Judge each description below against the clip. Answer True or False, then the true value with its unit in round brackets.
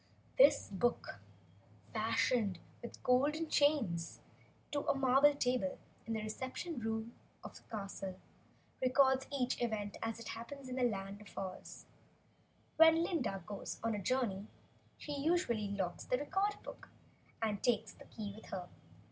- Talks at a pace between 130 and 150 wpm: True (145 wpm)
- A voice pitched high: True (235 Hz)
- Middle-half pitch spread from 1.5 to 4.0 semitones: False (5.0 semitones)